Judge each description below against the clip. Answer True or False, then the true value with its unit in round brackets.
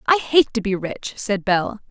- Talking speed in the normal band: False (220 wpm)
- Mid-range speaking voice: False (220 Hz)